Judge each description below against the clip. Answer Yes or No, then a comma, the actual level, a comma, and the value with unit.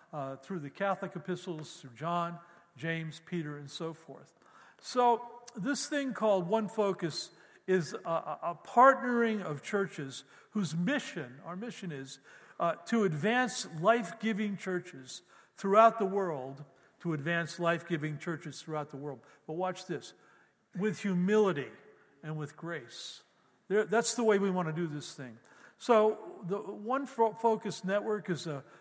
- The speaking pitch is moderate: Yes, medium, 180 Hz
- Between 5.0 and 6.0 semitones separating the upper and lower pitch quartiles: Yes, wide, 5.4 semitones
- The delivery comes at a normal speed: Yes, average, 150 wpm